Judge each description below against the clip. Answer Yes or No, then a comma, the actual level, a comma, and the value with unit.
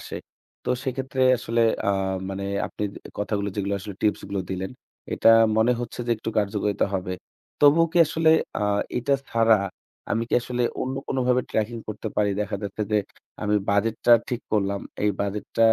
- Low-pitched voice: Yes, low, 110 Hz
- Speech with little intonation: No, average, 3.3 semitones